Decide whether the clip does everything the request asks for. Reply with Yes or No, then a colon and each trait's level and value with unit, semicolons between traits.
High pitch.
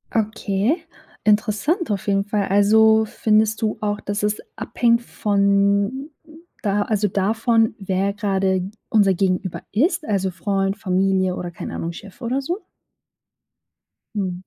Yes: high, 205 Hz